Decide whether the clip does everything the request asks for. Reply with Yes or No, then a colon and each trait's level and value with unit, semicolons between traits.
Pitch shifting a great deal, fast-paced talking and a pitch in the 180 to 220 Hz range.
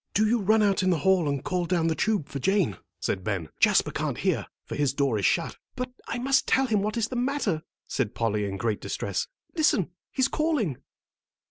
Yes: wide, 8.6 semitones; fast, 215 wpm; medium, 185 Hz